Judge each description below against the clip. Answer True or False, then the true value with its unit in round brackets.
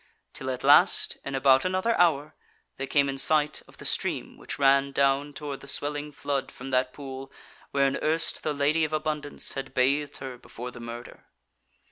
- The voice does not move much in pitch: True (1.9 semitones)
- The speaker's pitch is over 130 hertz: True (140 Hz)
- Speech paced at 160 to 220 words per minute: True (180 wpm)